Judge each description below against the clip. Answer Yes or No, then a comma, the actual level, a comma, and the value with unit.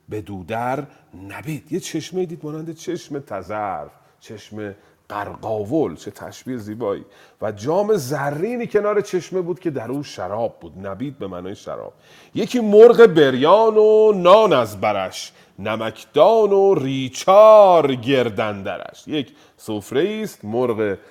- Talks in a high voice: No, medium, 140 Hz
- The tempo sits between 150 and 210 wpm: No, average, 125 wpm